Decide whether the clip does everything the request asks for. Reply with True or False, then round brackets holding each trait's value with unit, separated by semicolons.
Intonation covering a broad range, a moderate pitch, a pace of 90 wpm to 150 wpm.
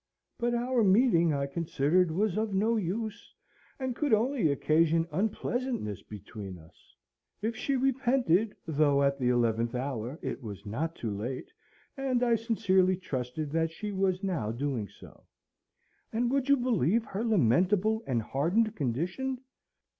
True (8.6 semitones; 180 Hz; 145 wpm)